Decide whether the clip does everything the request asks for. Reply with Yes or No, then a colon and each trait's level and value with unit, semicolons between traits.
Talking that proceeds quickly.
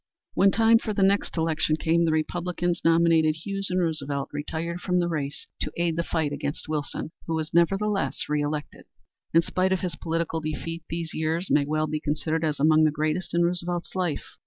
No: average, 190 wpm